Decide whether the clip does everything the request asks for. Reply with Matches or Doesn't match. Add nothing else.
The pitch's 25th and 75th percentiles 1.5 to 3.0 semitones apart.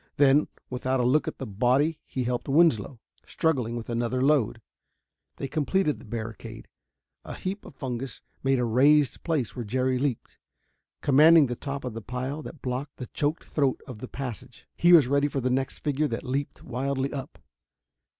Matches